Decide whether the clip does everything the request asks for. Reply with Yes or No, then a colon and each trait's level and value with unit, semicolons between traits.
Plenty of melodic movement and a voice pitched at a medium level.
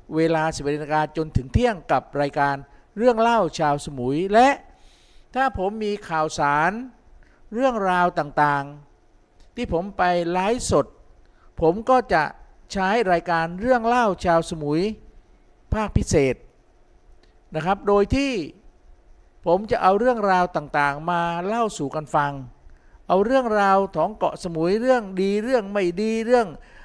Yes: wide, 6.3 semitones; medium, 180 Hz